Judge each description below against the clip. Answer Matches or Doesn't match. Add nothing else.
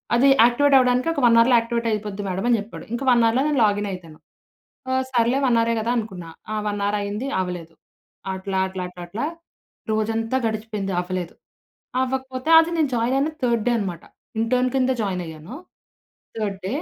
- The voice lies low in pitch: Doesn't match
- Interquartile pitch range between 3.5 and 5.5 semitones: Matches